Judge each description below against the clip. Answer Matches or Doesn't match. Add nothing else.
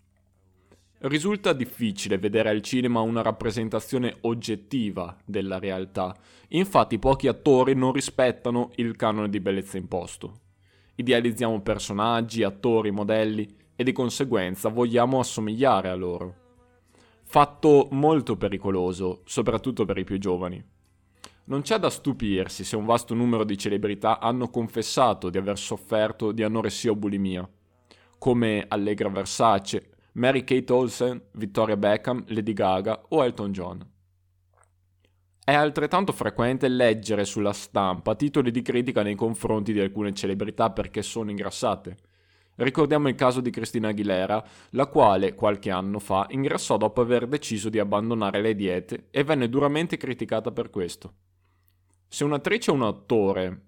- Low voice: Matches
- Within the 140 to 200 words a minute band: Doesn't match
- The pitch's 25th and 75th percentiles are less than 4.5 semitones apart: Matches